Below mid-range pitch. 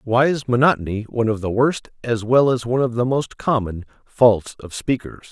Yes: low, 120 Hz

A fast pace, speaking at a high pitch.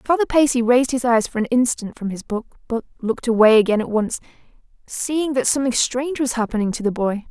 Yes: fast, 215 wpm; high, 240 Hz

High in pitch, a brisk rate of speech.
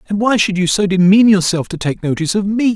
Yes: high, 195 Hz; fast, 260 wpm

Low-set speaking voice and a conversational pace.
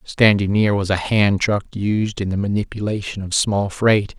Yes: low, 100 Hz; average, 185 wpm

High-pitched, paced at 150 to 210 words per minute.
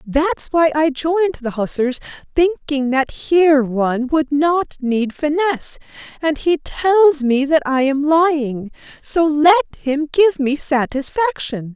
No: very high, 295 Hz; average, 140 wpm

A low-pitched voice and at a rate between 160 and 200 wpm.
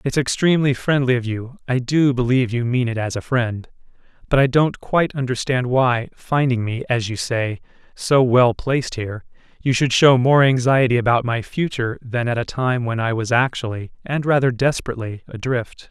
Yes: low, 125 Hz; average, 175 wpm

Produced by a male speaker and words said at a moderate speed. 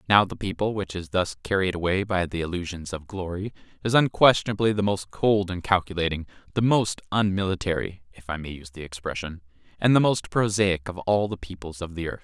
Yes: male; average, 195 wpm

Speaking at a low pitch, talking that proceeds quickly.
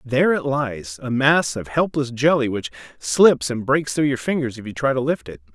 Yes: low, 130 Hz; fast, 225 wpm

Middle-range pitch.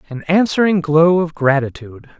Yes: medium, 160 Hz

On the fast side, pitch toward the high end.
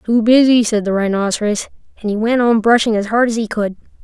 Yes: fast, 225 wpm; high, 220 Hz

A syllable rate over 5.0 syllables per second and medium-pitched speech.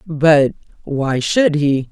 No: 2.7 syllables/s; medium, 150 Hz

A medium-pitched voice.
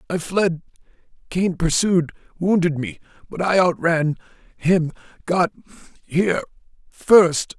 Yes: medium, 170 Hz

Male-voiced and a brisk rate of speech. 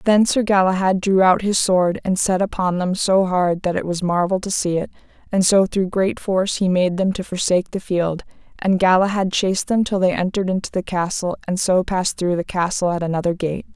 No: female; fast, 225 wpm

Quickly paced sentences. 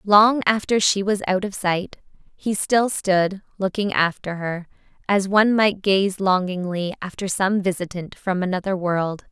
No: average, 155 wpm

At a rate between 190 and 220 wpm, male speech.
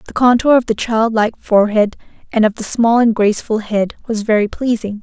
No: fast, 205 wpm; female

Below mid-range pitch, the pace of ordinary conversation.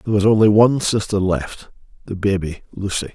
Yes: low, 100 Hz; average, 170 wpm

